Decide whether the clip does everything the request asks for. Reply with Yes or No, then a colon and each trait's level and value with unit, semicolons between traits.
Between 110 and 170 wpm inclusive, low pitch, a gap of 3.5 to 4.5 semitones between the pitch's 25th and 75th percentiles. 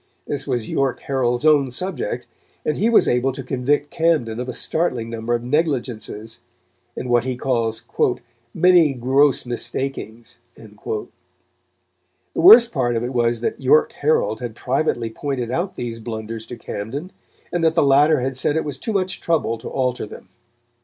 Yes: average, 165 wpm; low, 130 Hz; average, 4.2 semitones